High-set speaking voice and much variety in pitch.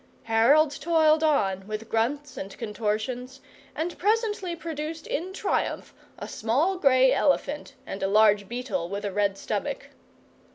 Yes: very high, 260 Hz; wide, 6.8 semitones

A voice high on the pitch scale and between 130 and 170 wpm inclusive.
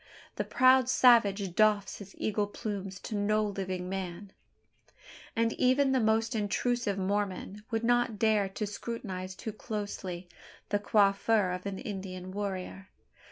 Yes: high, 205 Hz; slow, 135 wpm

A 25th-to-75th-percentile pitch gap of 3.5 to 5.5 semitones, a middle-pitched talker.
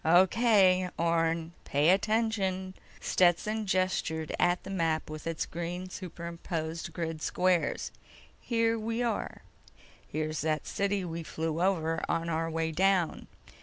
No: average, 2.7 semitones; medium, 175 Hz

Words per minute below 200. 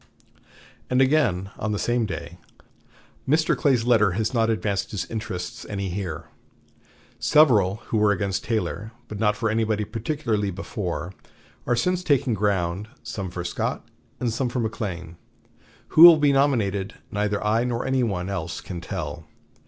Yes: average, 150 wpm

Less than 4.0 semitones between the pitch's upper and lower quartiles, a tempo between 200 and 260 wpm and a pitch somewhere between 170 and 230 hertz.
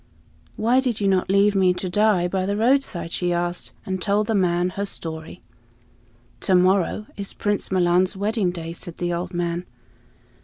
No: narrow, 2.6 semitones; average, 180 wpm; medium, 185 Hz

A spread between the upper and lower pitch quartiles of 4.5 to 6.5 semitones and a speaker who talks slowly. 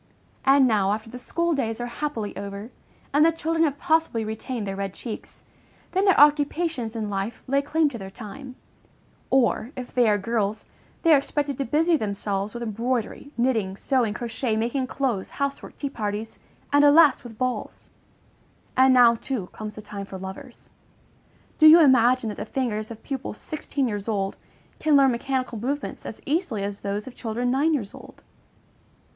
No: average, 4.8 semitones; average, 175 wpm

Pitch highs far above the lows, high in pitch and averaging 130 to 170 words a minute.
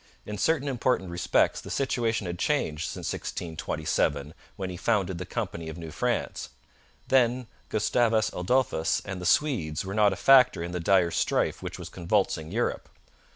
No: wide, 5.8 semitones; very low, 95 Hz; average, 160 wpm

